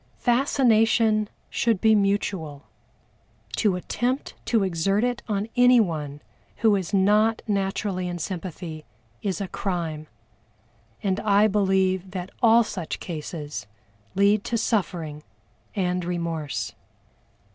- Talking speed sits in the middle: No, slow, 110 wpm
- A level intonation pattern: No, average, 3.7 semitones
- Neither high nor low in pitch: No, high, 195 Hz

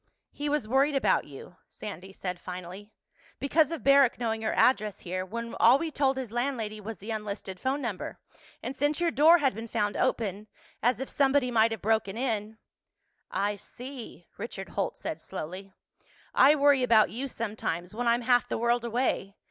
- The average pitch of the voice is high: Yes, high, 230 Hz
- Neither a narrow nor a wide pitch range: Yes, average, 4.6 semitones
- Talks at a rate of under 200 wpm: Yes, average, 175 wpm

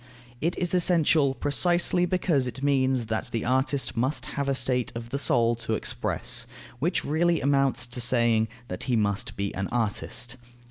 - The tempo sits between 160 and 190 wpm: Yes, average, 170 wpm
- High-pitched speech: No, low, 130 Hz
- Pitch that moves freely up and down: No, average, 3.9 semitones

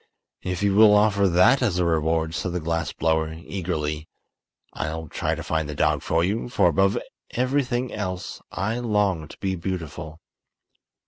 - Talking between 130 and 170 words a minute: Yes, average, 165 wpm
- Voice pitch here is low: Yes, very low, 90 Hz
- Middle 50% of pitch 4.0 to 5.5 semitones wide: Yes, average, 4.3 semitones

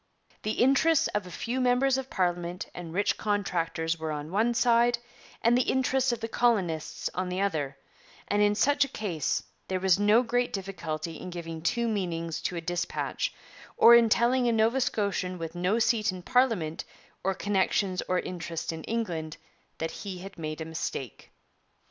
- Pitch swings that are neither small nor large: No, wide, 5.8 semitones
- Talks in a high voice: Yes, high, 195 Hz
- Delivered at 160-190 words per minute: Yes, average, 175 wpm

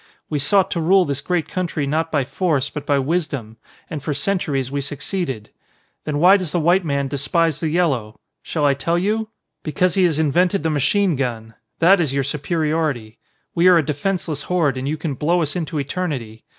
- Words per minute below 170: No, average, 195 wpm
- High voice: No, medium, 155 Hz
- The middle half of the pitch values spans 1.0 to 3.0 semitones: No, average, 4.0 semitones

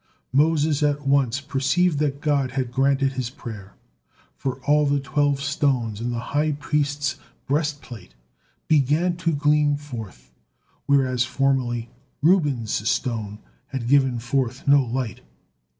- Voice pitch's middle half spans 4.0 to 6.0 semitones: No, average, 3.0 semitones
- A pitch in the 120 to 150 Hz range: Yes, medium, 140 Hz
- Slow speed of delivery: Yes, slow, 125 wpm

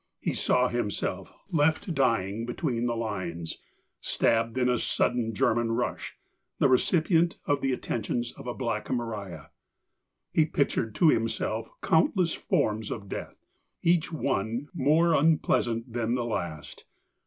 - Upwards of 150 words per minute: No, slow, 135 wpm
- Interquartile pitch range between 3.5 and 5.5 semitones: Yes, average, 4.6 semitones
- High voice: No, low, 120 Hz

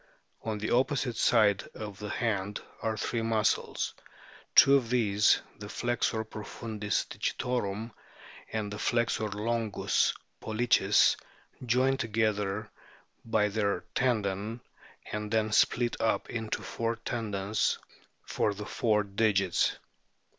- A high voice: No, low, 110 Hz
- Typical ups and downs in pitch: No, narrow, 2.0 semitones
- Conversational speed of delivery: No, slow, 110 wpm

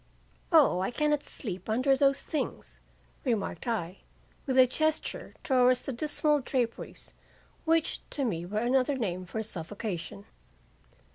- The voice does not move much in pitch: No, wide, 5.4 semitones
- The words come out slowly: Yes, slow, 130 wpm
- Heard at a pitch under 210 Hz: No, high, 245 Hz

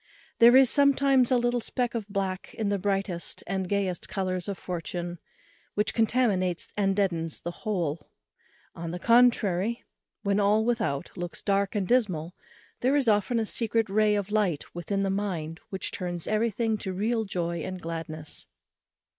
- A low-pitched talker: No, high, 200 Hz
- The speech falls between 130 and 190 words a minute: Yes, average, 160 wpm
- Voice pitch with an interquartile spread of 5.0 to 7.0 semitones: No, average, 4.0 semitones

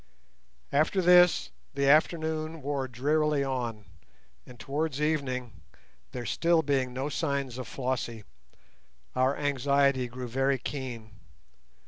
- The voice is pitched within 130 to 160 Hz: Yes, medium, 140 Hz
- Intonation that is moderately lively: Yes, average, 3.0 semitones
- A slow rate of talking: Yes, slow, 110 wpm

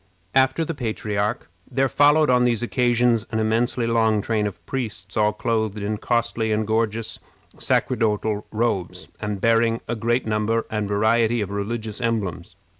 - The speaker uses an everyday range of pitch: No, narrow, 1.9 semitones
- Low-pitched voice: Yes, low, 110 Hz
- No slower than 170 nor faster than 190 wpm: No, average, 150 wpm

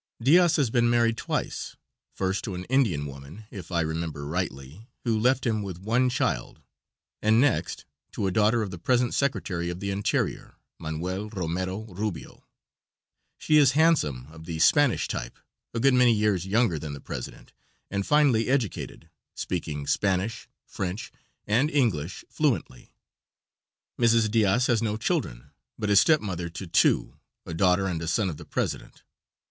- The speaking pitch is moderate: No, low, 100 Hz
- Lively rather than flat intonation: Yes, wide, 5.7 semitones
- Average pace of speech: Yes, average, 160 wpm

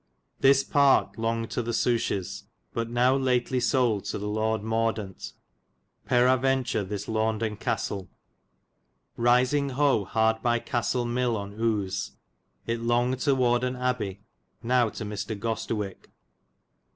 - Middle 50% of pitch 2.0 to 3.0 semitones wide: Yes, narrow, 2.6 semitones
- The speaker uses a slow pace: Yes, slow, 120 wpm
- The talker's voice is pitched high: No, low, 115 Hz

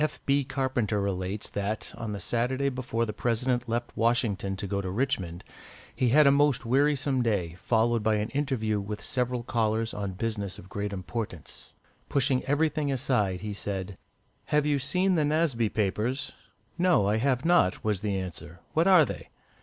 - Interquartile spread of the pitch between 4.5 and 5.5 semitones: Yes, average, 5.1 semitones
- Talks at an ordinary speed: Yes, average, 170 wpm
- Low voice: Yes, low, 115 Hz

